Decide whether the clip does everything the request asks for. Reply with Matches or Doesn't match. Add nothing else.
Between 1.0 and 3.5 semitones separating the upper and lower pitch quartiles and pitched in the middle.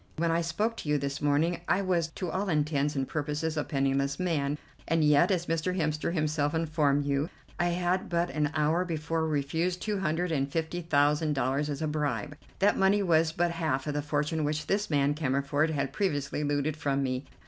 Matches